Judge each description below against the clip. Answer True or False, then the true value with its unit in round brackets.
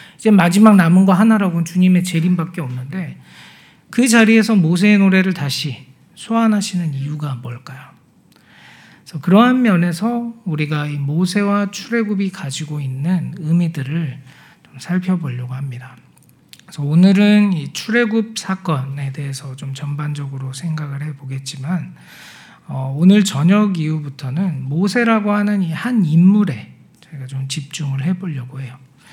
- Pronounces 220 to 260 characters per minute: False (305 characters per minute)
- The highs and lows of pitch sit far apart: True (5.8 semitones)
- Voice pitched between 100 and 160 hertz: False (170 Hz)